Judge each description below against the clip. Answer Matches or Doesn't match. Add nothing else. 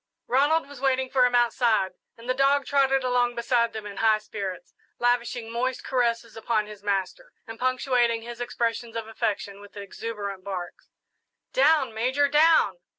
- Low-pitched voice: Doesn't match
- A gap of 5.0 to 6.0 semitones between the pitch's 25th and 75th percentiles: Doesn't match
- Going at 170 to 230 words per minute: Doesn't match